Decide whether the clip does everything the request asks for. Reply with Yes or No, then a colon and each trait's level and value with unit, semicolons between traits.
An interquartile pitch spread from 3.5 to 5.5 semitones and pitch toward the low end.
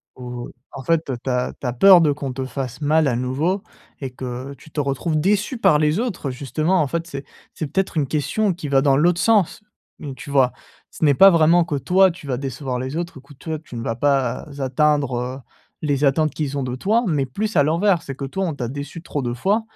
No: average, 4.1 semitones; medium, 145 Hz